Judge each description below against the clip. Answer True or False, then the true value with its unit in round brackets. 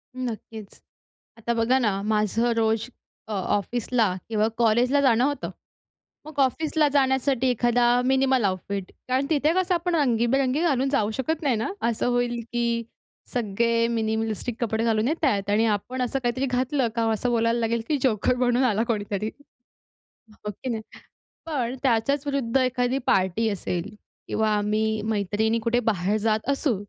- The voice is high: True (235 Hz)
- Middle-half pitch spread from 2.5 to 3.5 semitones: True (3.1 semitones)